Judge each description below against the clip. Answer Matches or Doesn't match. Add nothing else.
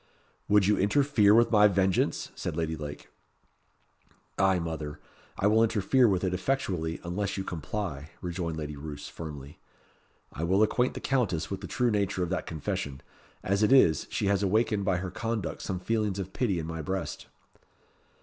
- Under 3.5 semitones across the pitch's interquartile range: Doesn't match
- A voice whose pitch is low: Matches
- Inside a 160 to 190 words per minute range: Matches